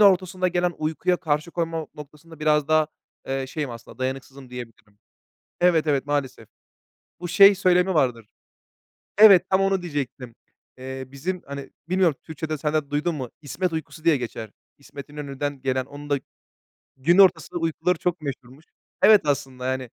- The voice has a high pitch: No, medium, 150 Hz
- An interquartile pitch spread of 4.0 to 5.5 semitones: Yes, average, 4.5 semitones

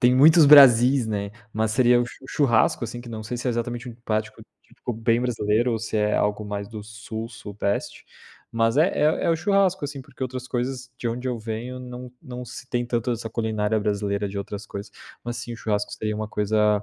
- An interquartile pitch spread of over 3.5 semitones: No, average, 2.8 semitones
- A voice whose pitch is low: Yes, low, 115 Hz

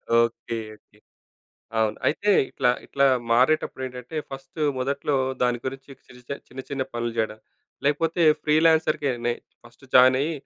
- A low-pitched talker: Yes, low, 130 Hz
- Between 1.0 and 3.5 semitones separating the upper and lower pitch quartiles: Yes, average, 3.1 semitones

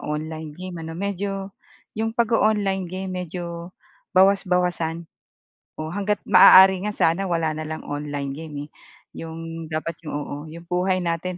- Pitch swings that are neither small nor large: Yes, average, 3.1 semitones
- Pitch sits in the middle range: Yes, medium, 175 Hz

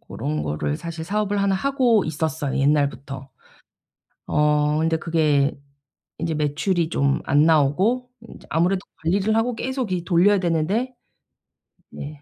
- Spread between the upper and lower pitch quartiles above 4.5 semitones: Yes, average, 5.3 semitones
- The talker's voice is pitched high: No, medium, 165 Hz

